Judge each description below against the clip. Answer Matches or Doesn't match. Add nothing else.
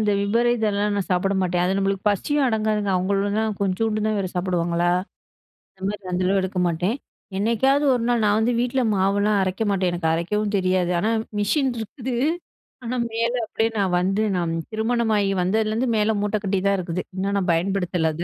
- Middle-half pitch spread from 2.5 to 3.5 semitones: Matches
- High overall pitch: Matches